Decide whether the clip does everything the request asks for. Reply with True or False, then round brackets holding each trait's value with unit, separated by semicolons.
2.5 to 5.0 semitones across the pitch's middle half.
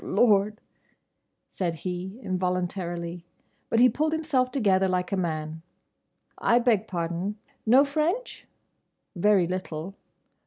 False (5.5 semitones)